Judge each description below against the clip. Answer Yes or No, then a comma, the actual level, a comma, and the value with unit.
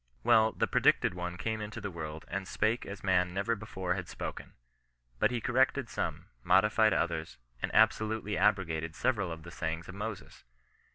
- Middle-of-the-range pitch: No, very low, 95 Hz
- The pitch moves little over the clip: No, average, 3.8 semitones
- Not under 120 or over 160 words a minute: No, average, 170 wpm